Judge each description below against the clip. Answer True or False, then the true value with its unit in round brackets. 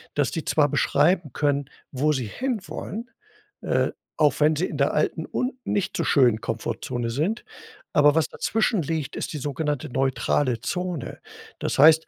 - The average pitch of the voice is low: False (150 Hz)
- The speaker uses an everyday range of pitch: True (3.8 semitones)